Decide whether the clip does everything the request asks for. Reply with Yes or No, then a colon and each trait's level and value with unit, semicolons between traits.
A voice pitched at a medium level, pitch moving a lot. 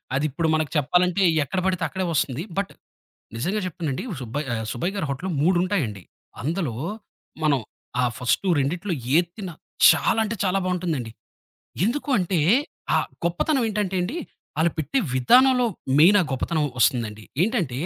Yes: medium, 175 Hz; wide, 5.7 semitones